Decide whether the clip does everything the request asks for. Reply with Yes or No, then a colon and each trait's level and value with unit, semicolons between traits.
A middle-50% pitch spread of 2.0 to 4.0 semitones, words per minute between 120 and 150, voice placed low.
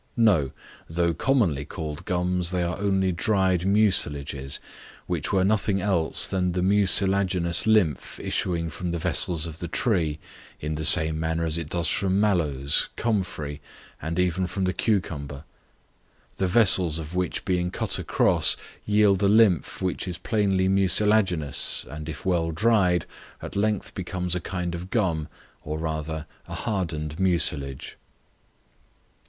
Yes: average, 3.4 semitones; average, 145 wpm; very low, 90 Hz